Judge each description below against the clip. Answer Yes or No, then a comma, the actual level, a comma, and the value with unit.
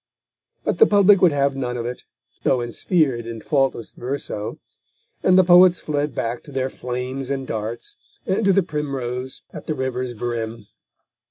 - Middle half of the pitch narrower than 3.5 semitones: No, average, 4.2 semitones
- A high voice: No, low, 130 Hz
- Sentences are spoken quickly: No, average, 165 wpm